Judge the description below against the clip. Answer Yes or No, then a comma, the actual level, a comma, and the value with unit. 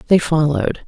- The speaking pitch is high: No, medium, 160 Hz